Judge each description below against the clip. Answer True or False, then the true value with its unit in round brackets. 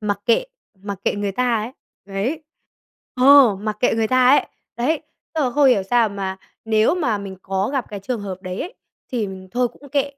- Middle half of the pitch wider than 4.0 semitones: True (4.4 semitones)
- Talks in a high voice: True (225 Hz)